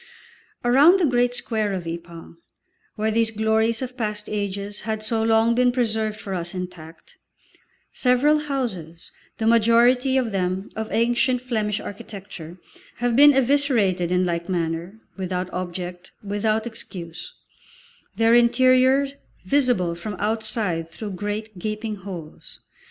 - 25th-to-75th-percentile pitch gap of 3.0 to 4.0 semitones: No, average, 4.7 semitones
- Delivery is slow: Yes, slow, 130 wpm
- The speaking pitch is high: Yes, high, 215 Hz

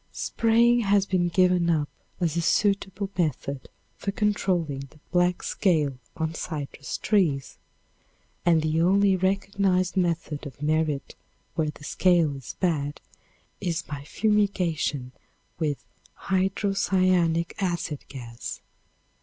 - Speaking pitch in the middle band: Yes, medium, 175 Hz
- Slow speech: Yes, slow, 110 wpm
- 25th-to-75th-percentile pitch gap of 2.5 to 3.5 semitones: No, average, 4.3 semitones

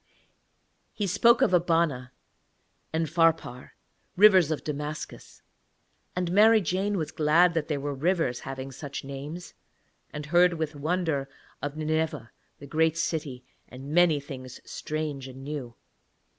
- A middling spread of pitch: Yes, average, 3.7 semitones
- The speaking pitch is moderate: Yes, medium, 155 Hz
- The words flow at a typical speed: No, slow, 130 wpm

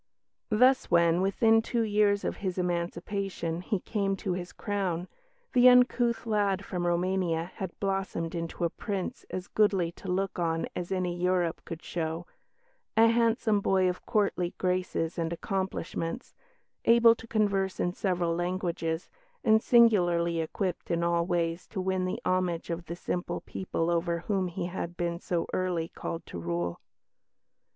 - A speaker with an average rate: Yes, average, 155 wpm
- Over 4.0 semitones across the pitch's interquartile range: No, average, 2.7 semitones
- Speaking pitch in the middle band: Yes, medium, 180 Hz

